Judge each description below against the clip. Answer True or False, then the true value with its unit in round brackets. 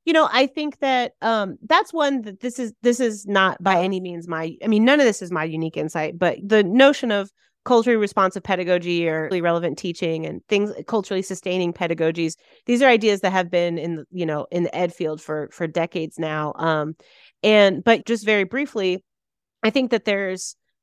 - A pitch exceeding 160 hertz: True (190 Hz)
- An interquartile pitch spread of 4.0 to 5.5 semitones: True (5.1 semitones)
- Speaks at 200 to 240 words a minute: True (205 wpm)